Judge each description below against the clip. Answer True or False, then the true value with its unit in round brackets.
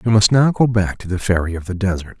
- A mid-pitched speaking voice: False (100 Hz)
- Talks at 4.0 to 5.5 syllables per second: False (6.2 syllables/s)